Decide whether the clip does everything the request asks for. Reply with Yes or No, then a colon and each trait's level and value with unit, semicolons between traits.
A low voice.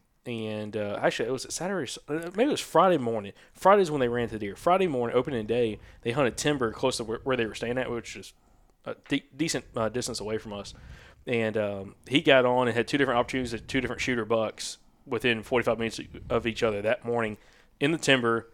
Yes: low, 120 Hz